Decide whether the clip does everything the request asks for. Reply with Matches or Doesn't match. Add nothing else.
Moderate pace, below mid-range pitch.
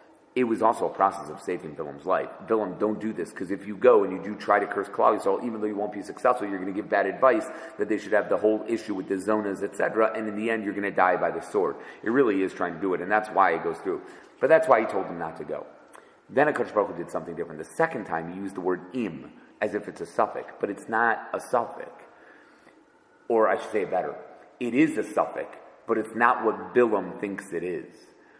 Doesn't match